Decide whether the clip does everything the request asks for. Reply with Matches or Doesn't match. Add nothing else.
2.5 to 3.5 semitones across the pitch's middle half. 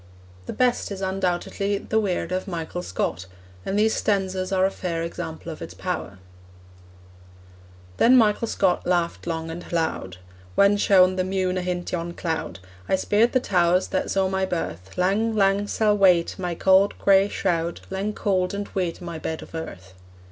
Matches